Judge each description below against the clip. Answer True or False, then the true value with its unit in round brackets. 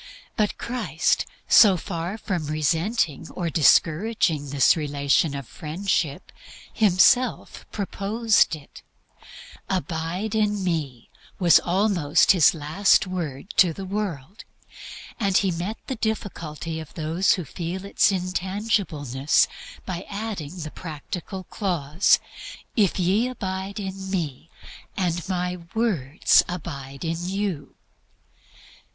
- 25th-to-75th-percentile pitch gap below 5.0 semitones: True (4.2 semitones)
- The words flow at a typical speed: False (110 wpm)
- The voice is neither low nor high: True (180 Hz)